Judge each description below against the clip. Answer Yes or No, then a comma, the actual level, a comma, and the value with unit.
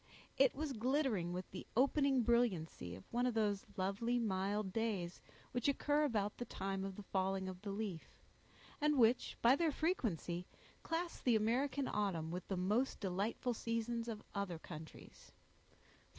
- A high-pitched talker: Yes, high, 215 Hz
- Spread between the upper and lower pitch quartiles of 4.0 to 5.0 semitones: Yes, average, 4.7 semitones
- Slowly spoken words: No, average, 155 wpm